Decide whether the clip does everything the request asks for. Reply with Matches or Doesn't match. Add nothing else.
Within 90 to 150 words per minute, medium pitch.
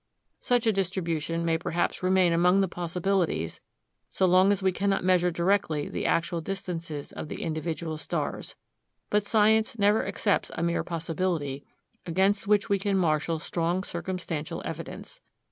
Matches